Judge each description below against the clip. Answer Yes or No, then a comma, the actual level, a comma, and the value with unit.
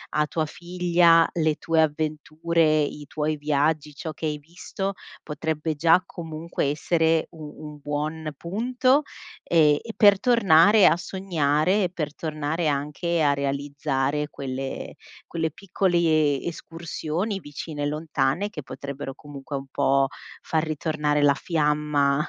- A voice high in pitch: No, medium, 155 Hz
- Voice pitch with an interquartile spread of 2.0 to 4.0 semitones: Yes, narrow, 2.5 semitones